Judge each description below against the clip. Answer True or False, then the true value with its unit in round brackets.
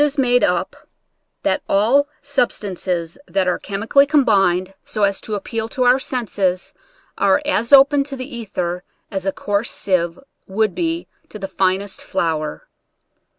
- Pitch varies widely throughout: True (5.8 semitones)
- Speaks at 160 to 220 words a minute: False (150 wpm)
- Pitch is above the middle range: True (205 Hz)